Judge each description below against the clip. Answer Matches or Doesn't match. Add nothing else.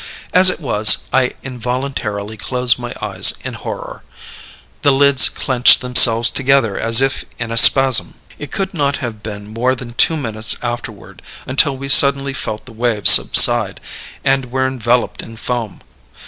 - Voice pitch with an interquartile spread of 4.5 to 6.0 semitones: Doesn't match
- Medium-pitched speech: Doesn't match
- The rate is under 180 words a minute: Matches